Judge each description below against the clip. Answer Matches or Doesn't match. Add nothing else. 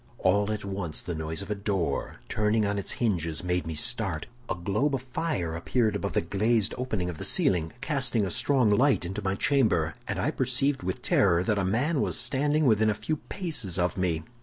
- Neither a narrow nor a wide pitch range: Doesn't match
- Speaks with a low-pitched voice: Matches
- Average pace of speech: Doesn't match